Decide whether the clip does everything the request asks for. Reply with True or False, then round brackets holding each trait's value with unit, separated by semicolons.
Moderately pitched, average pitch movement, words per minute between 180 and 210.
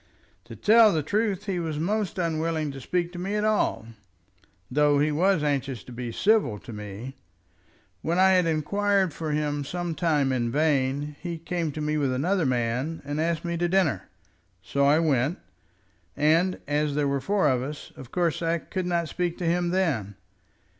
True (160 Hz; 4.1 semitones; 185 wpm)